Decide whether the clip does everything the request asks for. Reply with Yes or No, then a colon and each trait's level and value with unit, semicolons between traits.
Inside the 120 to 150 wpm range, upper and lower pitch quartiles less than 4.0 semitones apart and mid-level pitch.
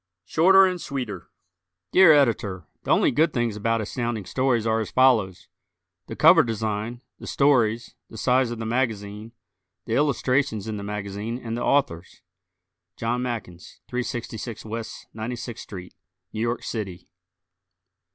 No: average, 140 wpm; average, 3.0 semitones; low, 115 Hz